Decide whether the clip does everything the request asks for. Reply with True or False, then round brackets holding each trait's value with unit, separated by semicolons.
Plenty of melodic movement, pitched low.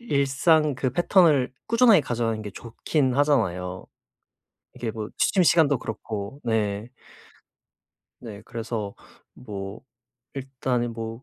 False (4.8 semitones; 120 Hz)